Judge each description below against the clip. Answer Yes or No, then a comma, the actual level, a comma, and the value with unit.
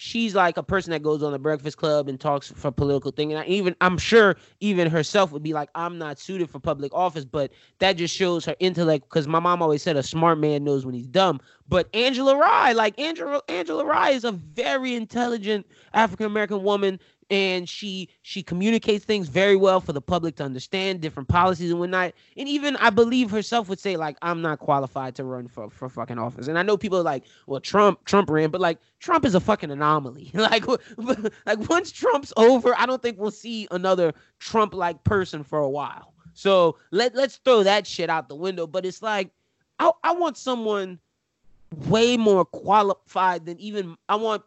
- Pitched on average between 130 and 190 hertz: Yes, medium, 185 Hz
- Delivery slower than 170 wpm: No, fast, 205 wpm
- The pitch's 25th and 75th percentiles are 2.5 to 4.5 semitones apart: No, wide, 5.5 semitones